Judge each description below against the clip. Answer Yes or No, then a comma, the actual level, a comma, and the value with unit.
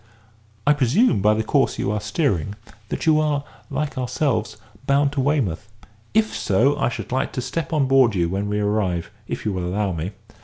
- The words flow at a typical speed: Yes, average, 195 wpm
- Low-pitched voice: Yes, low, 120 Hz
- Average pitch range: No, wide, 5.8 semitones